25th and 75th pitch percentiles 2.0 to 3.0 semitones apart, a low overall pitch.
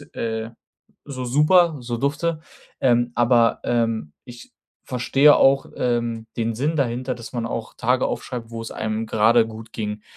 Yes: narrow, 2.4 semitones; low, 120 Hz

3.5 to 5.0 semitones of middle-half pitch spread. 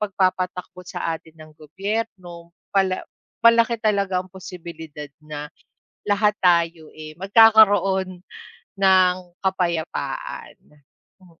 No: average, 2.9 semitones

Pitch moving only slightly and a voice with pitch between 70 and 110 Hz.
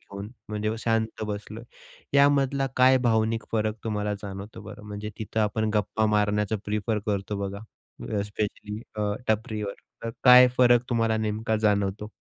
Yes: narrow, 1.4 semitones; low, 105 Hz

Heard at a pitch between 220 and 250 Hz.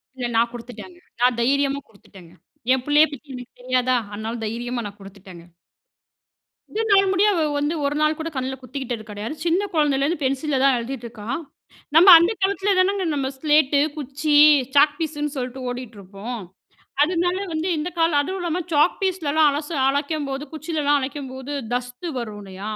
No: very high, 280 Hz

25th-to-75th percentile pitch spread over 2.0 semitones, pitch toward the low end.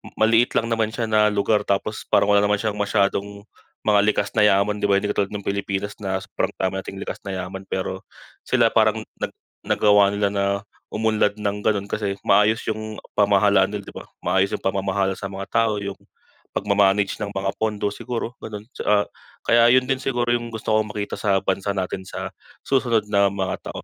No: narrow, 1.7 semitones; low, 105 Hz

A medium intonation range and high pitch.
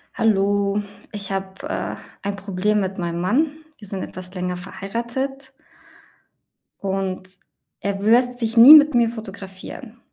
Yes: average, 3.5 semitones; high, 200 Hz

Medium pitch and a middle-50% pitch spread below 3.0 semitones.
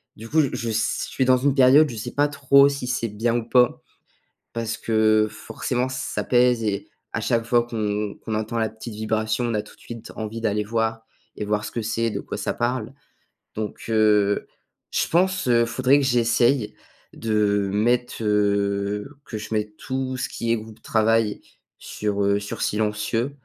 No: low, 115 Hz; narrow, 2.6 semitones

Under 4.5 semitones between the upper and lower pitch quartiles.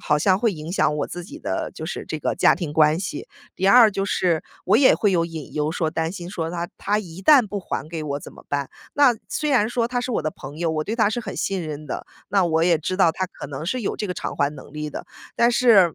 No: average, 5.0 semitones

